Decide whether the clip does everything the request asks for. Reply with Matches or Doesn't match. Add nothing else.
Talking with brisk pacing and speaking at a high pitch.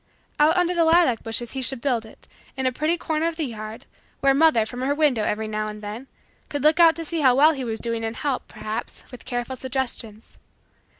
Matches